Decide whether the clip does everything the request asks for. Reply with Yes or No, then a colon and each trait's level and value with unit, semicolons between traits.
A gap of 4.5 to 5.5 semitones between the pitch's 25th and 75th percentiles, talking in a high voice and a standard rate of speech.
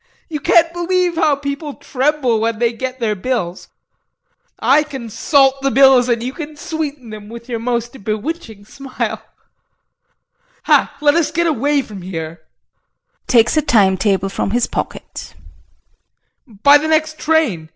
Yes: average, 5.2 semitones; very high, 260 Hz; average, 150 wpm